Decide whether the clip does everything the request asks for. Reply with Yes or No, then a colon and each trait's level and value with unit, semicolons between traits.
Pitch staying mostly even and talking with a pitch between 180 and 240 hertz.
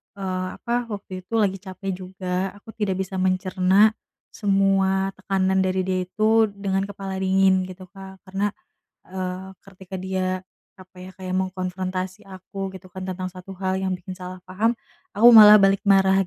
Yes: narrow, 1.0 semitones; high, 190 Hz